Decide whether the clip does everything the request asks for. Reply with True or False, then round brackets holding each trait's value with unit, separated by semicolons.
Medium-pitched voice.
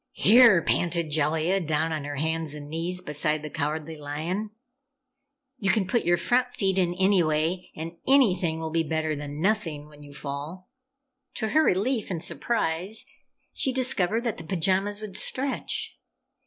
True (170 Hz)